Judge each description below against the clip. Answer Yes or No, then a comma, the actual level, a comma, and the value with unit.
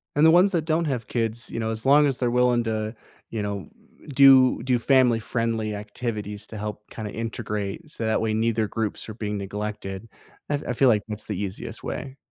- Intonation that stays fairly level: No, average, 3.2 semitones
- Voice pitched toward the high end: No, low, 115 Hz